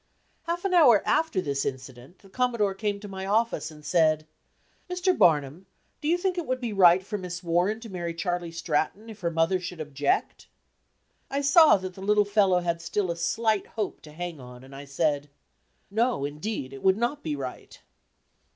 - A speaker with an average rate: Yes, average, 190 wpm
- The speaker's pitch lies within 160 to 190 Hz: Yes, medium, 185 Hz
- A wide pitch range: Yes, wide, 6.0 semitones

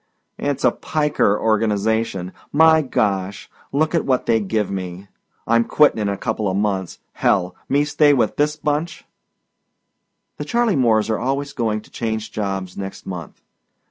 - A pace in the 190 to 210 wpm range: No, average, 145 wpm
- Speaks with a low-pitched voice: Yes, low, 110 Hz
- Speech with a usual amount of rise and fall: No, wide, 6.3 semitones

